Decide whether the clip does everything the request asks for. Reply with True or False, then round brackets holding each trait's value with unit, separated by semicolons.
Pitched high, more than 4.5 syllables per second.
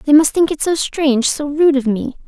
True (290 Hz; 5.2 syllables/s)